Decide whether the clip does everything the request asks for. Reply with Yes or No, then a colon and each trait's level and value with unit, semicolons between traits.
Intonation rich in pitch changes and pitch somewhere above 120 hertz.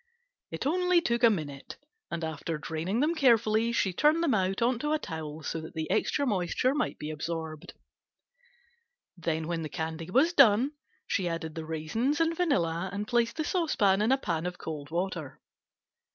Yes: wide, 8.3 semitones; high, 190 Hz